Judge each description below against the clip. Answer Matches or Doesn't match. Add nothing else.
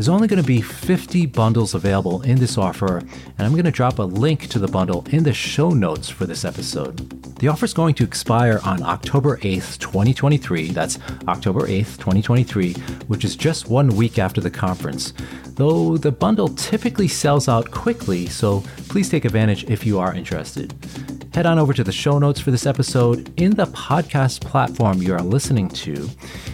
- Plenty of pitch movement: Matches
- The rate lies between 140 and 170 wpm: Doesn't match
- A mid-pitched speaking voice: Doesn't match